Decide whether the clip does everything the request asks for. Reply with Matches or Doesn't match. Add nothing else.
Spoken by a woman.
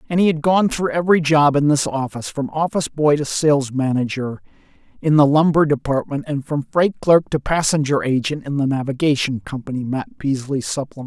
Doesn't match